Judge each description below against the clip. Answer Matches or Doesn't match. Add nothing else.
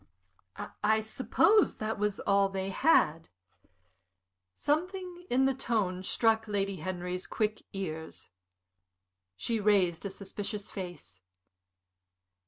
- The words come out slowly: Matches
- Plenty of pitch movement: Doesn't match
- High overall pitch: Matches